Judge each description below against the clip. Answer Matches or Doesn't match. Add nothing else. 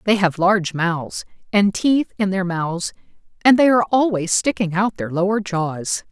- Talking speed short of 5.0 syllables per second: Matches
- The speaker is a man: Doesn't match